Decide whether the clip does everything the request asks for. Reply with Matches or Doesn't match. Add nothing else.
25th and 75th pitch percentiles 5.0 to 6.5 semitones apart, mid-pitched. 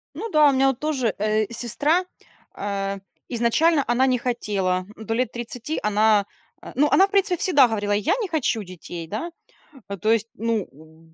Doesn't match